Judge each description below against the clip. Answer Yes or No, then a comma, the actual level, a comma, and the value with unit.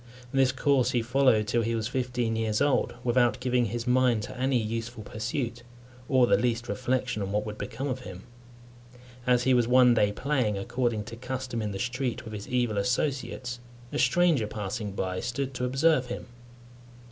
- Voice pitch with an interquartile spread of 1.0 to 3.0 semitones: Yes, average, 2.7 semitones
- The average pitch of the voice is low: Yes, low, 120 Hz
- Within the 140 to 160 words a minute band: No, average, 180 wpm